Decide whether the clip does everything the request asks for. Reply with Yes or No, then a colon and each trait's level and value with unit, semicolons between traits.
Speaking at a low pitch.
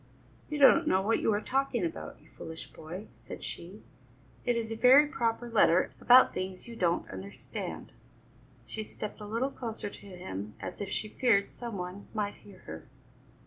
No: high, 210 Hz